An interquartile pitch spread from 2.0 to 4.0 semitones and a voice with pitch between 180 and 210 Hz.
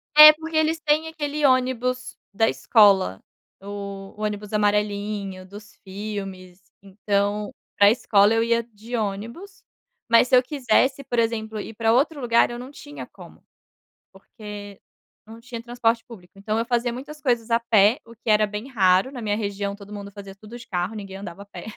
No: average, 3.4 semitones; high, 220 Hz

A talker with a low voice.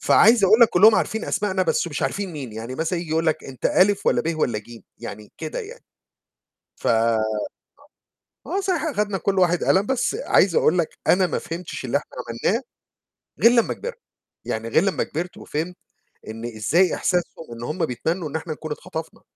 No: medium, 170 Hz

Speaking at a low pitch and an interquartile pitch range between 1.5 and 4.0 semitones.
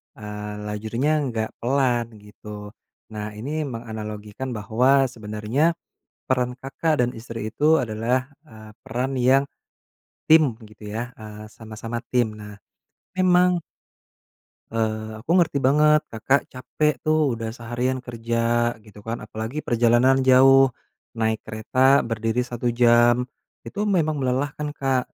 Yes: low, 120 Hz; average, 3.5 semitones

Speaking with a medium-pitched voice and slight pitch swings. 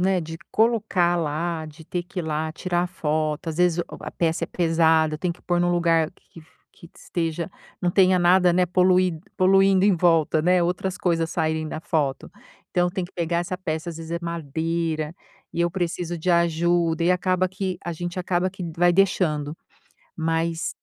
Yes: medium, 170 Hz; narrow, 1.9 semitones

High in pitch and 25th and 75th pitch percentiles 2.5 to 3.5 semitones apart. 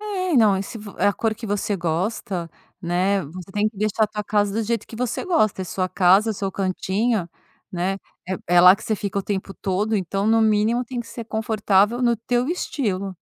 Yes: high, 205 Hz; average, 3.0 semitones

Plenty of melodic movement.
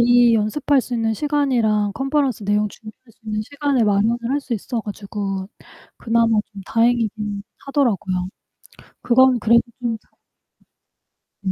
No: average, 3.3 semitones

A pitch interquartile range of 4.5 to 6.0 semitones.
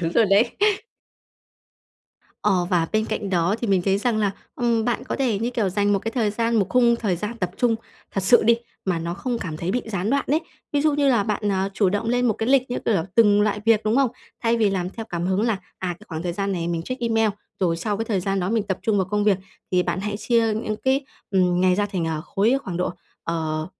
No: average, 3.9 semitones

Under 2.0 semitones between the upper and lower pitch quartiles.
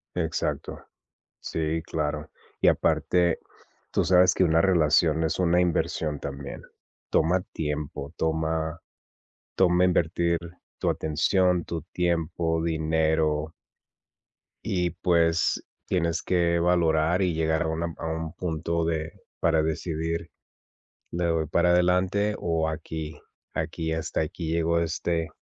Yes: narrow, 1.5 semitones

